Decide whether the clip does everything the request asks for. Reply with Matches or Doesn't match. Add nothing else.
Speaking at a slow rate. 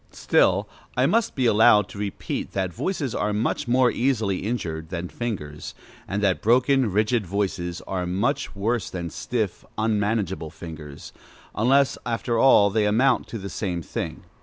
Doesn't match